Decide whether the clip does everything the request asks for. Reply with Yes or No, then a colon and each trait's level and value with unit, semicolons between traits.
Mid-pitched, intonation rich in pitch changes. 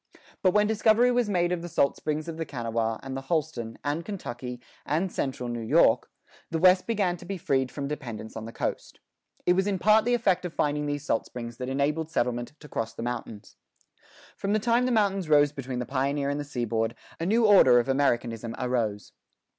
Yes: medium, 145 Hz; wide, 7.0 semitones